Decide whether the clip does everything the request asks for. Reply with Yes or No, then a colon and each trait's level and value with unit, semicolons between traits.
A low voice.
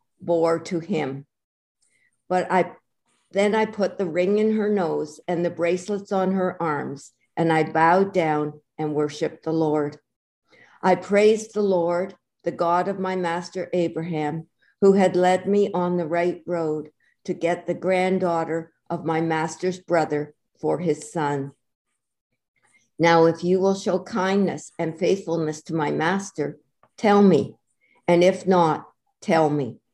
No: medium, 170 Hz